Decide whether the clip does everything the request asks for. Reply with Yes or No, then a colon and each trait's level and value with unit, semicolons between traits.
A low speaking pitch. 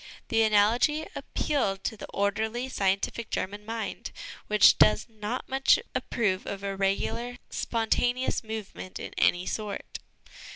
No: high, 215 Hz